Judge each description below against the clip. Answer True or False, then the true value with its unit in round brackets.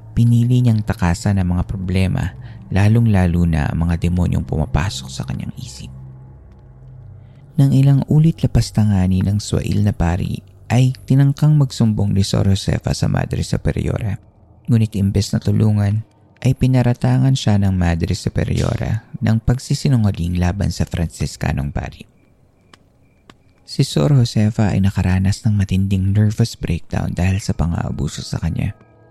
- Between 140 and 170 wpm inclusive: False (130 wpm)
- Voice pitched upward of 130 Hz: False (105 Hz)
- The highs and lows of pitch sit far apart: False (4.5 semitones)